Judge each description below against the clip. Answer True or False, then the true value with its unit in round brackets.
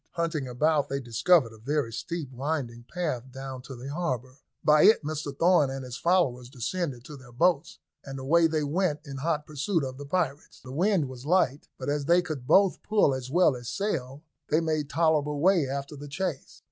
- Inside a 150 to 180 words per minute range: False (195 wpm)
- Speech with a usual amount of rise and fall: True (4.2 semitones)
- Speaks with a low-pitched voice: False (145 Hz)